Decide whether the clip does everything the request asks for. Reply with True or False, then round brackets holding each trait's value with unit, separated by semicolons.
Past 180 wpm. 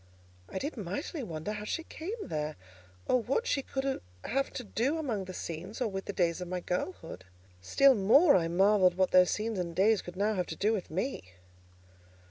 True (200 wpm)